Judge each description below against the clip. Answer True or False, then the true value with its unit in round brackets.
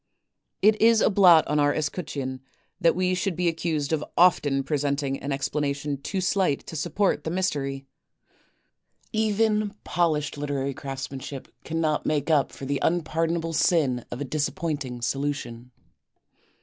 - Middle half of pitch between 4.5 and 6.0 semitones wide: False (3.9 semitones)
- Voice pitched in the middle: True (150 Hz)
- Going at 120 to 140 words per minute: True (135 wpm)